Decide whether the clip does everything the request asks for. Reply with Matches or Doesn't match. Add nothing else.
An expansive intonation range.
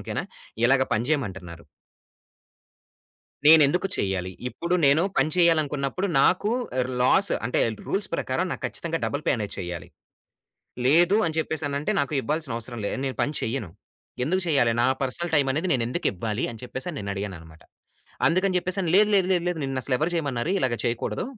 Matches